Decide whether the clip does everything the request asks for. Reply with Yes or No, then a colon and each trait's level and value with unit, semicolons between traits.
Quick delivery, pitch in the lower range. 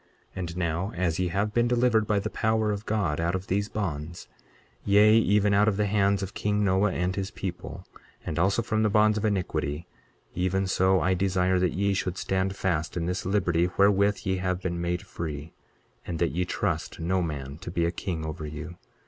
Yes: fast, 210 wpm; very low, 95 Hz